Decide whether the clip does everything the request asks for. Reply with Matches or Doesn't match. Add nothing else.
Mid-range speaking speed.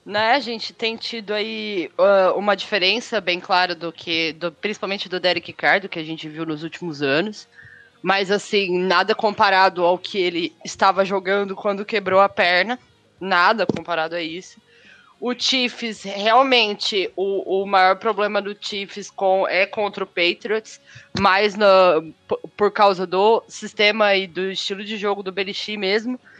Matches